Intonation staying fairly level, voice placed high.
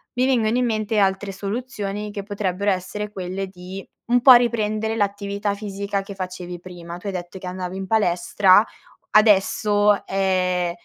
Yes: narrow, 2.2 semitones; high, 200 Hz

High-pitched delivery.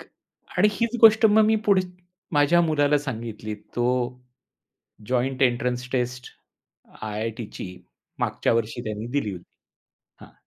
No: low, 125 Hz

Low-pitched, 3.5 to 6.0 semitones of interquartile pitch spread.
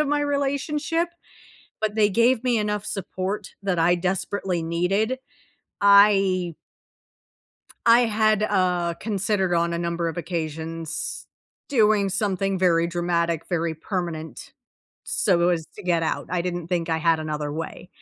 No: medium, 185 Hz; average, 3.8 semitones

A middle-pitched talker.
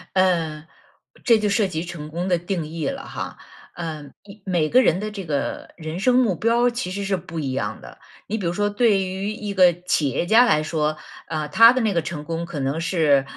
Yes: medium, 175 Hz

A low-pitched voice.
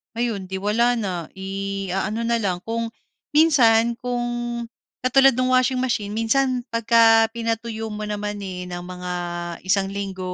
No: high, 225 Hz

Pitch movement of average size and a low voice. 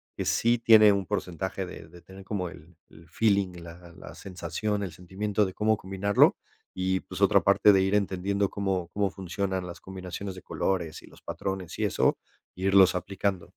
No: narrow, 1.8 semitones; very low, 95 Hz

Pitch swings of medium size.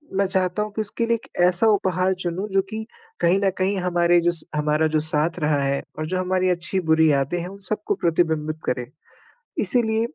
Yes: average, 3.5 semitones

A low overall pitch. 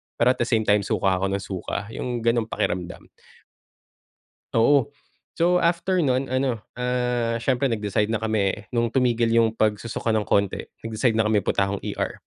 Yes: low, 115 Hz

